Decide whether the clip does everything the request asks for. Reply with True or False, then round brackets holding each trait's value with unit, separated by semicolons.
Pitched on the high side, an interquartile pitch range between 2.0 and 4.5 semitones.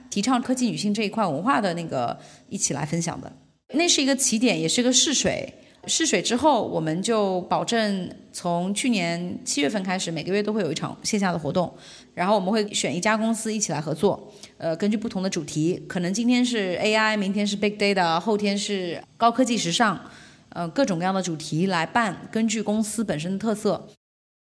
True (205 Hz; 4.0 semitones)